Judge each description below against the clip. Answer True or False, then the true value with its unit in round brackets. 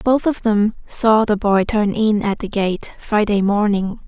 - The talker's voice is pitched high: True (210 Hz)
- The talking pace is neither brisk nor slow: True (190 wpm)